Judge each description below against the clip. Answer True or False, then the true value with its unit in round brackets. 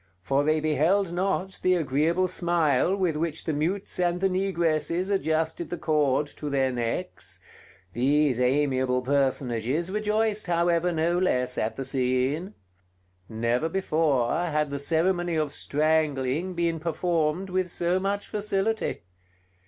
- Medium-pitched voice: True (160 Hz)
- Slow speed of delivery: True (130 wpm)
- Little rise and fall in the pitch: False (4.4 semitones)